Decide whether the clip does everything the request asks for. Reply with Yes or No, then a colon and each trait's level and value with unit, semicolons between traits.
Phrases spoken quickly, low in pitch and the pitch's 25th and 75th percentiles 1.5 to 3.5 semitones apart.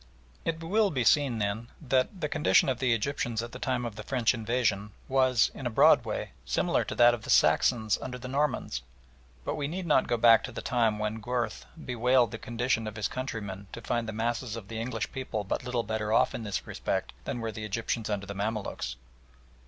Yes: fast, 215 wpm; low, 120 Hz; average, 2.8 semitones